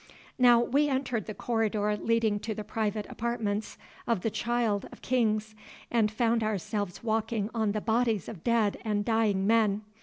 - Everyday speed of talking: Yes, average, 160 wpm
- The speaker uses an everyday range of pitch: No, narrow, 1.9 semitones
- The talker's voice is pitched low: No, high, 220 Hz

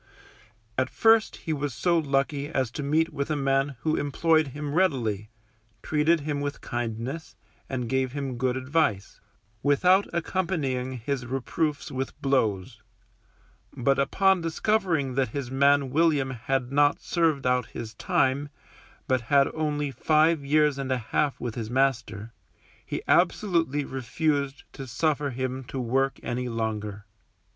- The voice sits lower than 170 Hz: Yes, medium, 140 Hz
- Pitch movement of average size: Yes, average, 3.3 semitones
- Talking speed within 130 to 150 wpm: Yes, average, 140 wpm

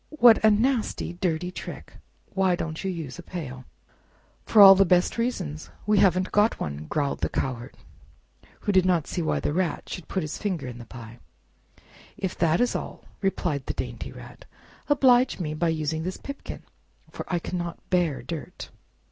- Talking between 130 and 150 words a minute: No, average, 175 wpm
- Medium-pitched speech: Yes, medium, 175 Hz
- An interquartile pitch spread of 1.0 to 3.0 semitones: No, average, 4.1 semitones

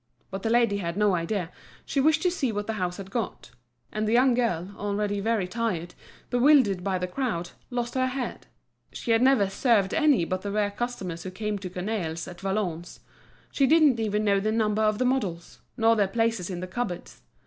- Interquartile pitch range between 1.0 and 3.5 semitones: No, average, 4.3 semitones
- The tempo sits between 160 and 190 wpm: No, fast, 205 wpm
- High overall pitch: Yes, high, 210 Hz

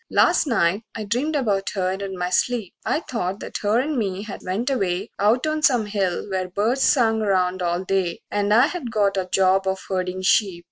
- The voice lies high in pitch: Yes, high, 200 Hz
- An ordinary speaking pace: No, fast, 215 wpm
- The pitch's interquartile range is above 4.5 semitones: No, average, 3.9 semitones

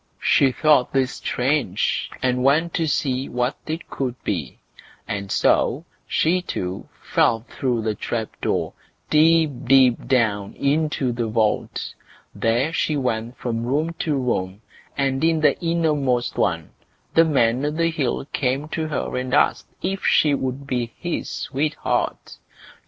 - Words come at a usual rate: Yes, average, 145 wpm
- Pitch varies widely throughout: No, average, 4.4 semitones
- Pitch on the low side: Yes, low, 130 Hz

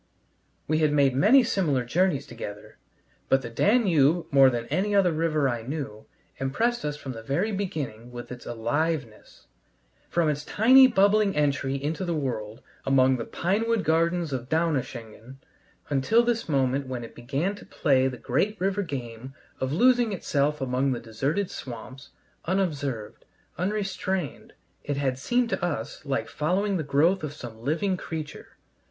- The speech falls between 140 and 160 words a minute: Yes, average, 155 wpm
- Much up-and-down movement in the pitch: Yes, wide, 6.3 semitones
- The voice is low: No, medium, 145 Hz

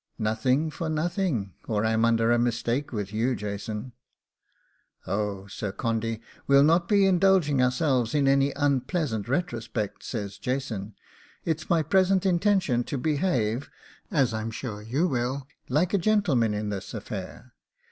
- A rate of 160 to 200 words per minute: No, average, 140 wpm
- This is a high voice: No, low, 125 Hz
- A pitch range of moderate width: No, wide, 6.0 semitones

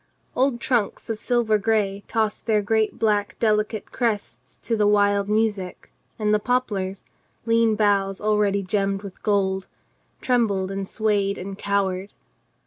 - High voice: Yes, high, 210 Hz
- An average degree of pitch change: No, narrow, 1.9 semitones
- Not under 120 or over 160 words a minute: Yes, average, 140 wpm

